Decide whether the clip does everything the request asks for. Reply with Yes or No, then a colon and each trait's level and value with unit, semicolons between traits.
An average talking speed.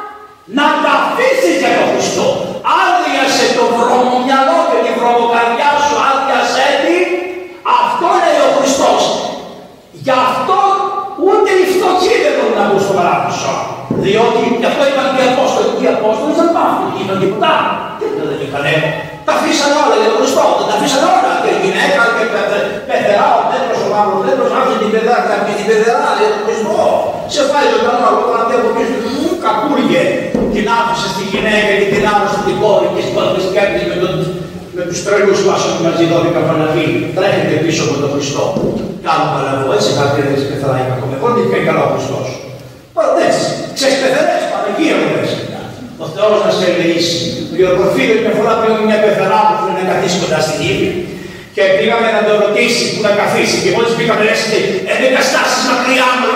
Yes: average, 125 wpm